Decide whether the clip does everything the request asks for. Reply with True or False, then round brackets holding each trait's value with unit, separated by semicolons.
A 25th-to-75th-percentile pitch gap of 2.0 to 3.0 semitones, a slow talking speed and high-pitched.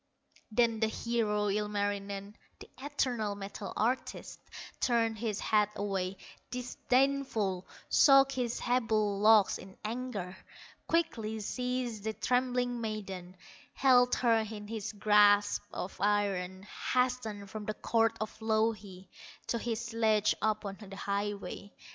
True (2.7 semitones; 120 wpm; 215 Hz)